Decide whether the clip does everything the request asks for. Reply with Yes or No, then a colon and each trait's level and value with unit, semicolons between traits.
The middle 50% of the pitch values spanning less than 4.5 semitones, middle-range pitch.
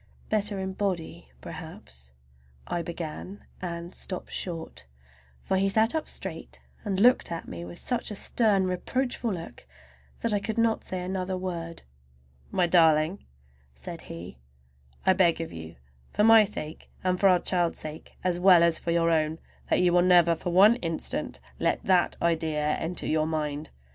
Yes: average, 3.3 semitones; medium, 175 Hz